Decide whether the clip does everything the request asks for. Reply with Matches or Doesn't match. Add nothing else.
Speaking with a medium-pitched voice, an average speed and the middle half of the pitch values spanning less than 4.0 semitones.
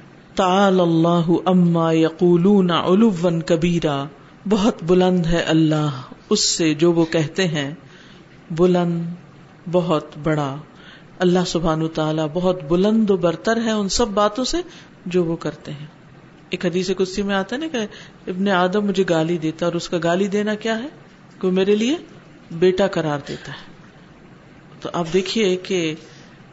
Matches